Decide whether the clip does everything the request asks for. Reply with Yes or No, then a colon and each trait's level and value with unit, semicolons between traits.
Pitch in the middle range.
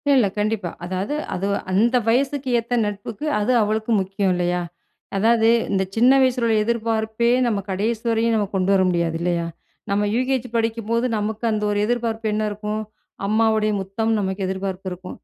No: high, 215 Hz